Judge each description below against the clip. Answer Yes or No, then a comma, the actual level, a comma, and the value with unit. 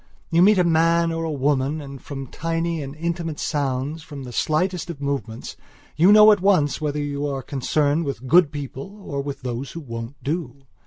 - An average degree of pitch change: Yes, average, 3.3 semitones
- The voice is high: No, medium, 150 Hz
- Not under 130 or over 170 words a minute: No, average, 195 wpm